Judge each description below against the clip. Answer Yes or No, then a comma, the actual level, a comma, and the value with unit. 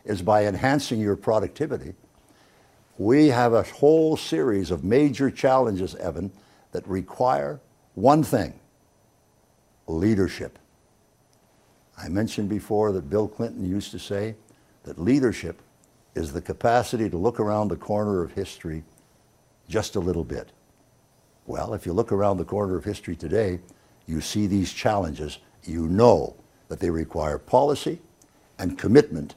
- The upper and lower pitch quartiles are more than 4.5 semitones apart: No, average, 3.8 semitones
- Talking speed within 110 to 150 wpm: Yes, slow, 135 wpm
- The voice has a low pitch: Yes, low, 105 Hz